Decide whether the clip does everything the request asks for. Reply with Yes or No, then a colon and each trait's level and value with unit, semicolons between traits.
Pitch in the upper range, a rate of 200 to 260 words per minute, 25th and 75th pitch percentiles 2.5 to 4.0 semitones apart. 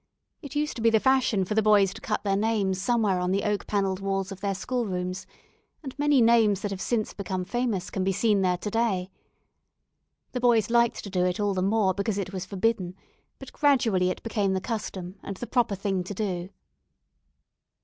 Yes: high, 200 Hz; fast, 205 wpm; average, 3.2 semitones